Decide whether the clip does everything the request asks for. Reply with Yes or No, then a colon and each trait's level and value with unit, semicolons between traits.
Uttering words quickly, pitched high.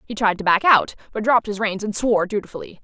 Yes: fast, 255 wpm; high, 210 Hz